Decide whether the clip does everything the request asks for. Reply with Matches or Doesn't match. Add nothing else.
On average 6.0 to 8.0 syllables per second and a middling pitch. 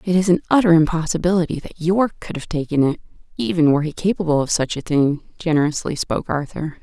Matches